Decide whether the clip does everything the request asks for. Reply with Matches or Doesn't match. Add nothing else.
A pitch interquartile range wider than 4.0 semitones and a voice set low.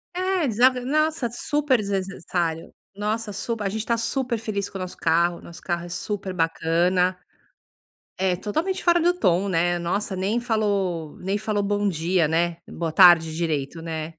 Doesn't match